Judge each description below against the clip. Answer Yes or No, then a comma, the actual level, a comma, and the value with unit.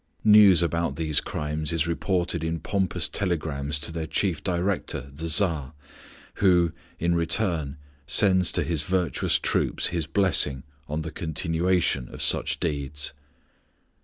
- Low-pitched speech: Yes, very low, 85 Hz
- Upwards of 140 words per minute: No, slow, 135 wpm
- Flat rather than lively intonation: No, average, 3.0 semitones